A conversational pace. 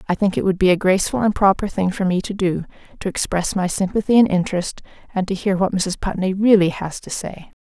No: fast, 235 wpm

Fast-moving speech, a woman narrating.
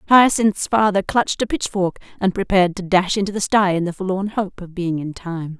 Yes: fast, 215 wpm; female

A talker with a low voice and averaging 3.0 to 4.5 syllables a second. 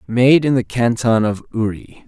Yes: low, 115 Hz; 4.4 syllables/s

